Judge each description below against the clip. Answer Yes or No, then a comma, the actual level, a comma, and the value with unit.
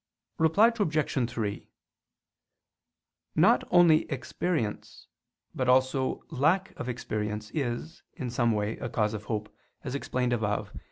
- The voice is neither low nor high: No, low, 125 Hz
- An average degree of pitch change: No, wide, 6.1 semitones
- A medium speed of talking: No, slow, 125 wpm